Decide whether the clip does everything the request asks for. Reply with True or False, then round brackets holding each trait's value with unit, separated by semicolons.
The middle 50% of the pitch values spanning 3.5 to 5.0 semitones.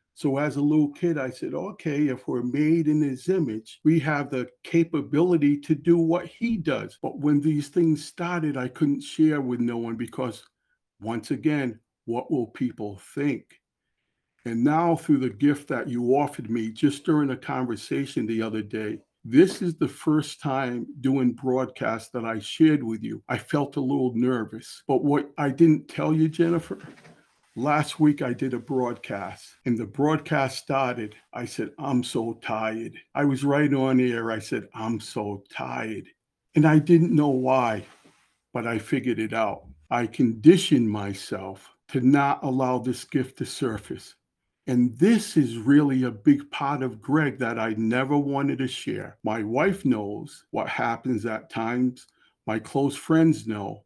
True (4.2 semitones)